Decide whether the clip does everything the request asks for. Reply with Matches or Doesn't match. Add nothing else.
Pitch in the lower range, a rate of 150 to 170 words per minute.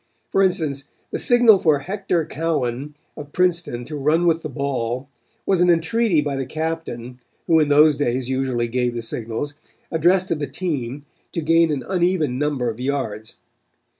Doesn't match